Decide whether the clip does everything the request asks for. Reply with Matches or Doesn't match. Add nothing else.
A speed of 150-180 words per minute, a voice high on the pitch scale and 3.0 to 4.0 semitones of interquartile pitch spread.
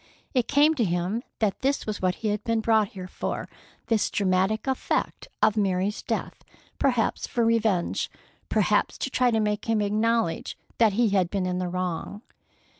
Matches